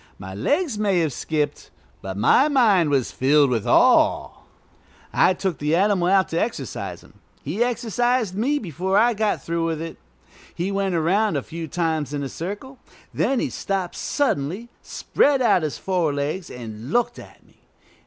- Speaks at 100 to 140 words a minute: No, average, 165 wpm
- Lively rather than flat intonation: Yes, wide, 6.4 semitones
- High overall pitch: No, medium, 180 Hz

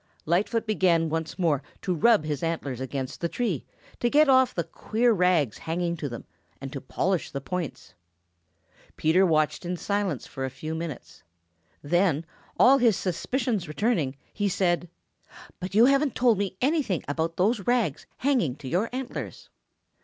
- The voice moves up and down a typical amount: No, wide, 6.4 semitones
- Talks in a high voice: No, medium, 180 Hz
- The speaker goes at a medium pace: Yes, average, 160 wpm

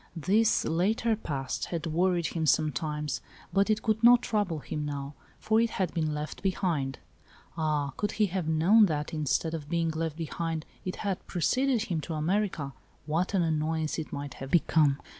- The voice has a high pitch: No, medium, 165 Hz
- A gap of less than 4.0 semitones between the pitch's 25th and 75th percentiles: No, average, 4.3 semitones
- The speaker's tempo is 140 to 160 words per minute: No, average, 175 wpm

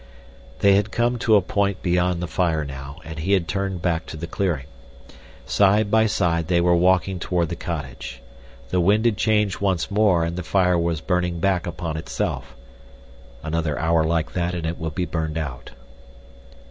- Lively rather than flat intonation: No, average, 3.3 semitones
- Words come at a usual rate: Yes, average, 180 wpm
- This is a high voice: No, very low, 85 Hz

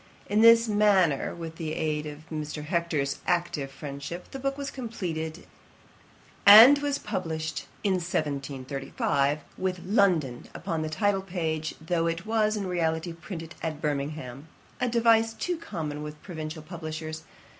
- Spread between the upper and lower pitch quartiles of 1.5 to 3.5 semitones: No, average, 4.6 semitones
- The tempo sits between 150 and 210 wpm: No, average, 140 wpm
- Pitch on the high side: No, medium, 165 Hz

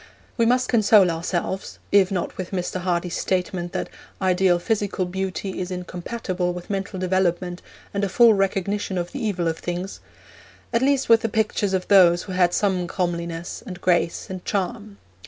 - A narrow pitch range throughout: Yes, narrow, 2.3 semitones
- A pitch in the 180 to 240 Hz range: Yes, medium, 185 Hz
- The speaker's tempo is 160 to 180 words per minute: Yes, average, 170 wpm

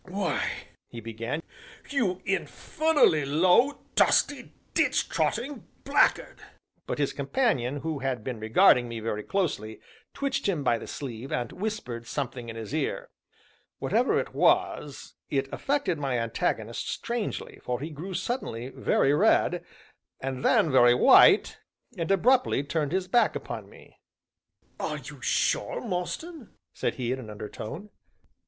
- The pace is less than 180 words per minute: Yes, average, 140 wpm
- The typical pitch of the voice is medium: Yes, medium, 145 Hz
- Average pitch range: No, wide, 8.3 semitones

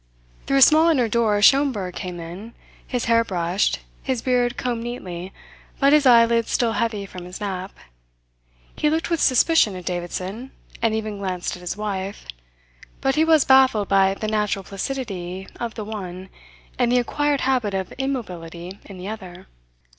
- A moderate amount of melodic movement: Yes, average, 5.0 semitones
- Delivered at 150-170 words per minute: Yes, average, 165 wpm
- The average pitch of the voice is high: Yes, high, 215 Hz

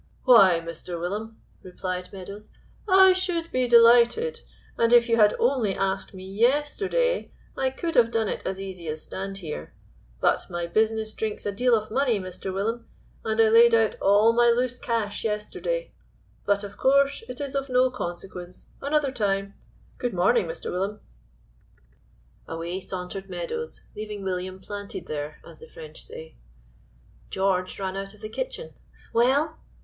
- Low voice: No, high, 215 Hz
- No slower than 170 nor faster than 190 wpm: No, average, 155 wpm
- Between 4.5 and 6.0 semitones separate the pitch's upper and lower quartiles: Yes, average, 4.9 semitones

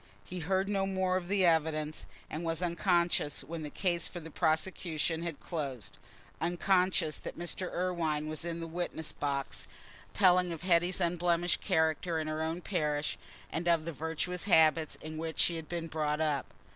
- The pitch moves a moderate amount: No, narrow, 2.1 semitones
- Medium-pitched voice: Yes, medium, 165 Hz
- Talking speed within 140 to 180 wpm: Yes, average, 170 wpm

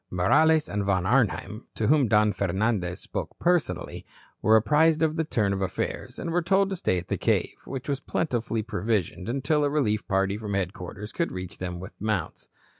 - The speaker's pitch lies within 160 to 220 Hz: No, low, 110 Hz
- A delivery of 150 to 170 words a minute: No, average, 190 wpm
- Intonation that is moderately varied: No, wide, 7.4 semitones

